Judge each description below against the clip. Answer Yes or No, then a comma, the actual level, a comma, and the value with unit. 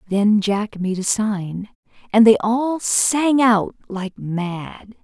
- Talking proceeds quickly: No, average, 145 wpm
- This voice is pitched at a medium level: No, high, 210 Hz